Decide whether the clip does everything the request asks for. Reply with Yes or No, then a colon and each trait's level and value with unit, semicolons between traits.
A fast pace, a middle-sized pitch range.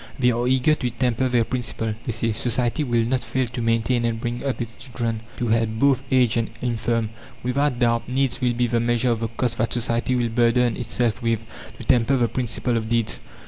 No: fast, 215 wpm; narrow, 1.5 semitones